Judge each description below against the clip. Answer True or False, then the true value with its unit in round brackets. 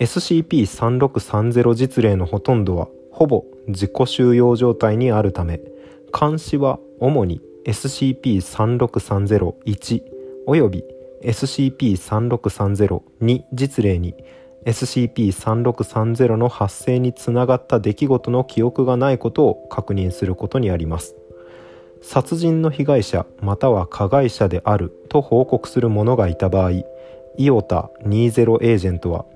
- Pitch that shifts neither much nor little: True (4.6 semitones)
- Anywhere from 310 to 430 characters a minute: False (225 characters per minute)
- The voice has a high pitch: False (120 Hz)